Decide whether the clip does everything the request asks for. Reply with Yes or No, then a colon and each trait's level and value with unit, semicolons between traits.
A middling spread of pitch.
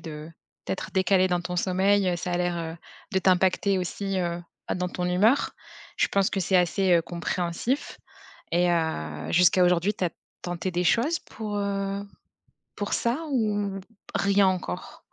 No: narrow, 2.3 semitones